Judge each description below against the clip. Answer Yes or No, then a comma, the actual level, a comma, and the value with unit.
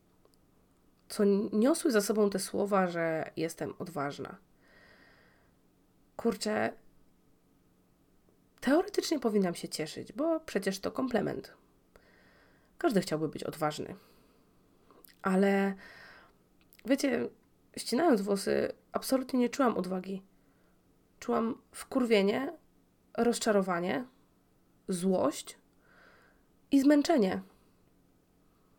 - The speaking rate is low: Yes, slow, 75 wpm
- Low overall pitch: No, high, 205 Hz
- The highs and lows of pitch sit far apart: Yes, wide, 5.8 semitones